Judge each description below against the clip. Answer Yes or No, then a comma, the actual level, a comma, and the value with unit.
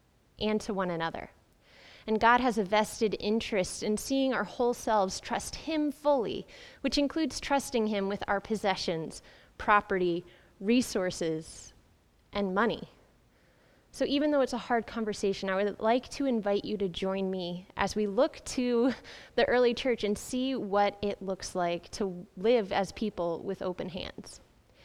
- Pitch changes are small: No, average, 4.1 semitones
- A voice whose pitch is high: Yes, high, 210 Hz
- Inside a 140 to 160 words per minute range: Yes, average, 155 wpm